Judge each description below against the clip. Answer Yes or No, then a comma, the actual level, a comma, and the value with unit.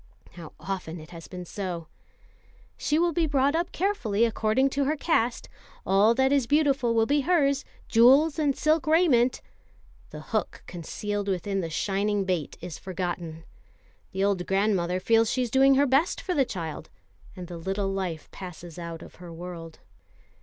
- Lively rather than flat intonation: Yes, wide, 7.4 semitones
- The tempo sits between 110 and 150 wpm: No, average, 165 wpm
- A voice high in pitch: Yes, high, 205 Hz